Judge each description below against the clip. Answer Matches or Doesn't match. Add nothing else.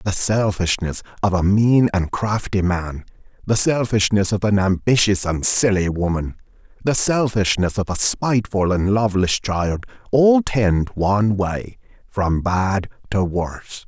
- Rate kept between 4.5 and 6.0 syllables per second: Doesn't match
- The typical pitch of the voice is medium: Doesn't match